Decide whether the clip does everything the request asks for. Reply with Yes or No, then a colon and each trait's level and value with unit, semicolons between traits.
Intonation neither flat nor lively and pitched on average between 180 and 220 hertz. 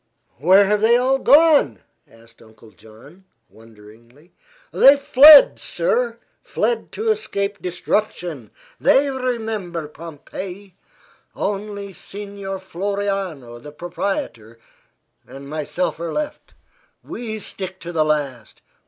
No: wide, 6.6 semitones; medium, 185 Hz